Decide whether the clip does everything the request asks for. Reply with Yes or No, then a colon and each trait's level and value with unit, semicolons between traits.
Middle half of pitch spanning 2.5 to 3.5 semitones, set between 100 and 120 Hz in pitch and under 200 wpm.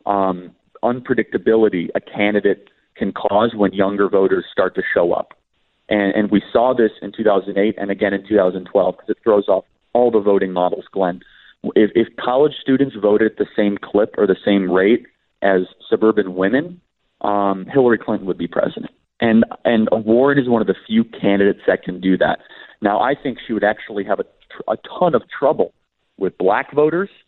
Yes: average, 2.8 semitones; low, 105 Hz; average, 185 wpm